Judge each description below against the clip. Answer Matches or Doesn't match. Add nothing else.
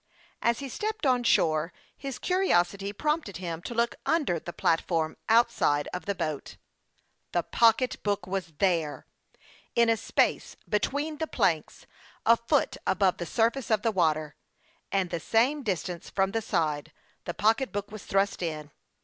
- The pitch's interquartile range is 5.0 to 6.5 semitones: Matches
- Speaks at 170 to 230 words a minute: Doesn't match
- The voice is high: Matches